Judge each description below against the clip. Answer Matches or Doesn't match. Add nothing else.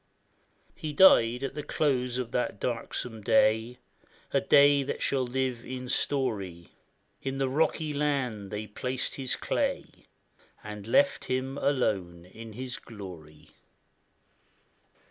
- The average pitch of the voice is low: Matches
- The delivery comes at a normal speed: Doesn't match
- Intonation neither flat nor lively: Matches